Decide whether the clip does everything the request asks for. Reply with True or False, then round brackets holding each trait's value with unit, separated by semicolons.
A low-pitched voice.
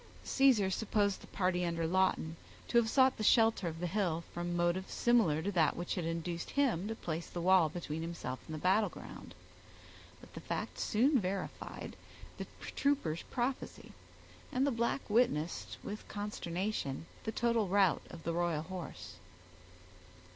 False (185 Hz)